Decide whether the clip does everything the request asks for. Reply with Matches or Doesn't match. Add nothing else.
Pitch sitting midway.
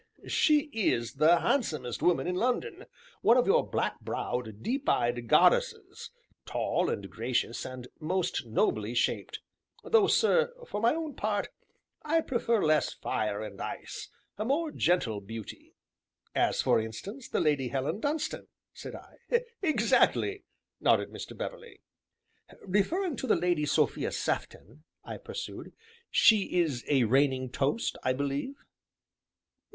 Matches